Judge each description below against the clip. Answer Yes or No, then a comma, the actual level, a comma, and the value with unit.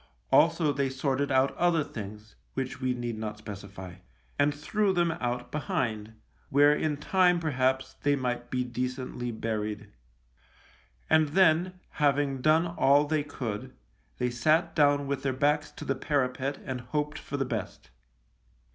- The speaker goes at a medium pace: Yes, average, 145 wpm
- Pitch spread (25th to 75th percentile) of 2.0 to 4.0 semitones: Yes, average, 3.4 semitones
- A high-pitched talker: No, low, 135 Hz